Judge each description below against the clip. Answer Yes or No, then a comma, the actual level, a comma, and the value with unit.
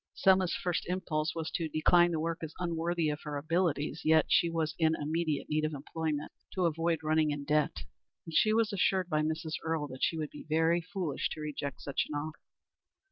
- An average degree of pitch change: No, narrow, 2.0 semitones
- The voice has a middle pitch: Yes, medium, 160 Hz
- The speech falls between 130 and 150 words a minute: No, average, 200 wpm